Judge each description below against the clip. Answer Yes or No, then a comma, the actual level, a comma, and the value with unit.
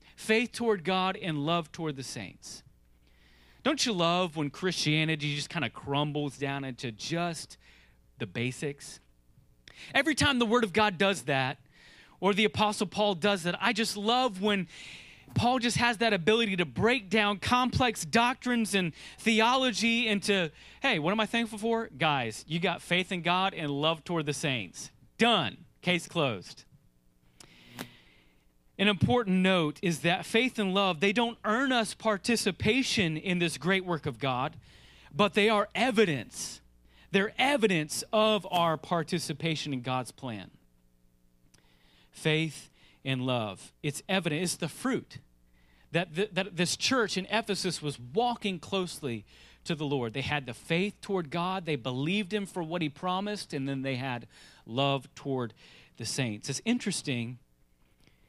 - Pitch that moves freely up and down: Yes, wide, 7.5 semitones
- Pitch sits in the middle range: Yes, medium, 170 Hz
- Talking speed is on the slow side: No, average, 150 wpm